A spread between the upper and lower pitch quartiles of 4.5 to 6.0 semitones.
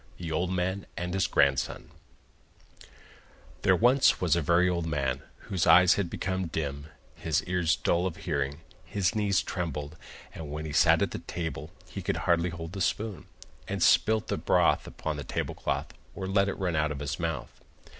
No: average, 3.4 semitones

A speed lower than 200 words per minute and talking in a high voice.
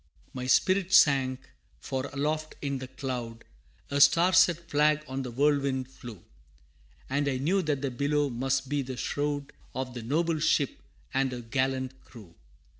No: average, 160 wpm; low, 135 Hz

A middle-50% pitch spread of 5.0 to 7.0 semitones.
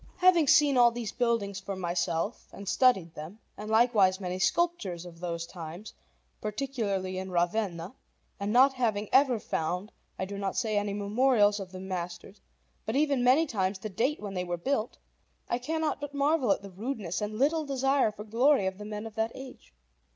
Yes: average, 5.3 semitones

